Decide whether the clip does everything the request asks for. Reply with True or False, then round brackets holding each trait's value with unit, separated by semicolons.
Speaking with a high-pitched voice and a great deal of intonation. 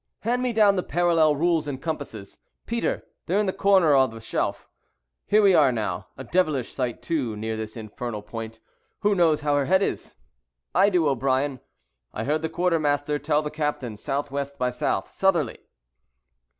False (150 Hz; 5.7 semitones)